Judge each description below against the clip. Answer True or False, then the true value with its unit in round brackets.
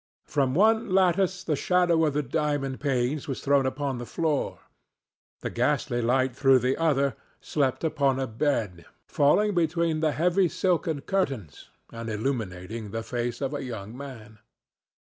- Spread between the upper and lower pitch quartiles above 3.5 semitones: True (4.8 semitones)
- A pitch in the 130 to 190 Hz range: True (140 Hz)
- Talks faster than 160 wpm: False (150 wpm)